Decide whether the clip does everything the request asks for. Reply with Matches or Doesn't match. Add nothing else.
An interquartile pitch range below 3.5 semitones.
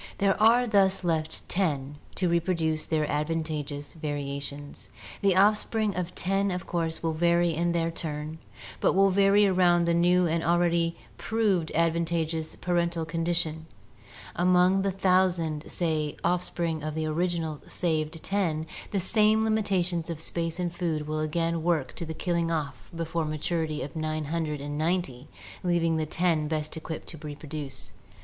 Matches